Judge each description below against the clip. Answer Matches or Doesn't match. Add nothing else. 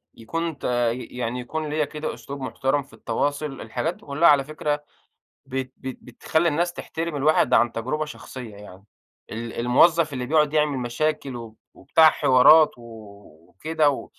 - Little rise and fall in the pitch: Doesn't match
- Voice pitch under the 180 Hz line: Matches